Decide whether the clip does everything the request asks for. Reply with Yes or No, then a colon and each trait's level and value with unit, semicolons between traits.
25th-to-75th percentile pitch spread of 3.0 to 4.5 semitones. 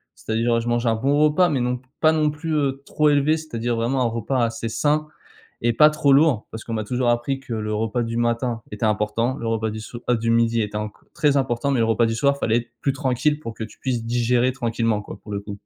Yes: average, 3.3 semitones